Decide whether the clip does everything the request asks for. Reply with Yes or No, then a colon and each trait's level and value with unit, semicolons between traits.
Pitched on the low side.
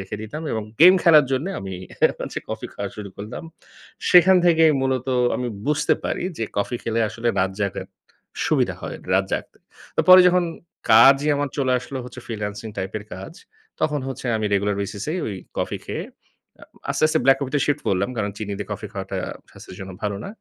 Yes: low, 115 Hz